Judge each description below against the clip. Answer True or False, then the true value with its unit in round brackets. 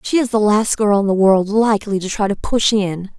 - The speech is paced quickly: True (265 wpm)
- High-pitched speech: True (205 Hz)